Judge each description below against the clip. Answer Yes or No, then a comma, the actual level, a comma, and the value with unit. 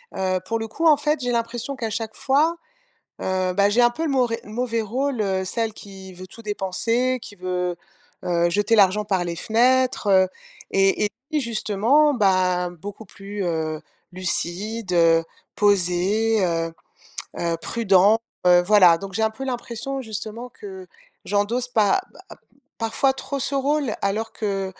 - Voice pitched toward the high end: Yes, high, 210 Hz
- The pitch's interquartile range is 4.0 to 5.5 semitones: Yes, average, 4.4 semitones